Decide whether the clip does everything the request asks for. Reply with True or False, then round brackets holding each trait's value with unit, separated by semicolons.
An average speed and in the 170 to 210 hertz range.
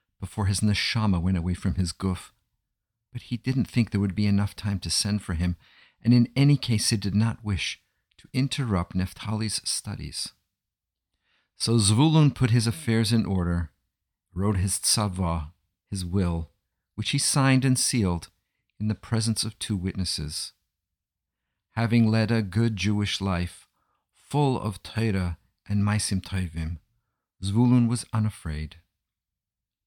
False (145 wpm; 100 Hz)